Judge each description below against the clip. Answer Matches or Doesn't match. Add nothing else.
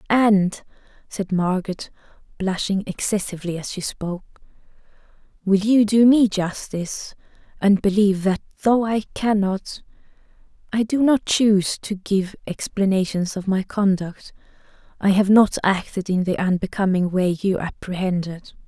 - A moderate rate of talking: Doesn't match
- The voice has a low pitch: Doesn't match